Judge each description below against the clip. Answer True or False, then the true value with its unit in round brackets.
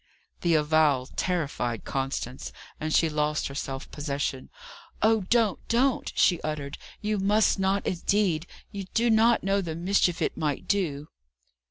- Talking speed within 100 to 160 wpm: True (145 wpm)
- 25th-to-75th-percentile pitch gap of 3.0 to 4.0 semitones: False (5.4 semitones)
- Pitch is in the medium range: True (170 Hz)